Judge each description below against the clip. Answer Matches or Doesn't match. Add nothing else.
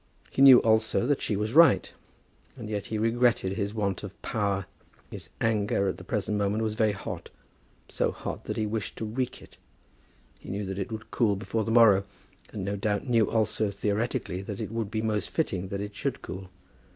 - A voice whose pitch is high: Doesn't match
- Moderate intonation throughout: Doesn't match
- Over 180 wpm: Matches